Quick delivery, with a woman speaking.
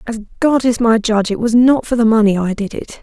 Yes: fast, 280 wpm; female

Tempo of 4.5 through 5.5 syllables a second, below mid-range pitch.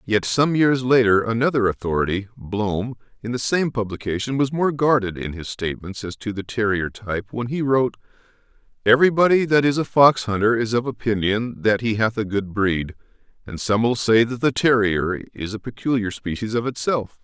Yes: 5.3 syllables/s; low, 115 Hz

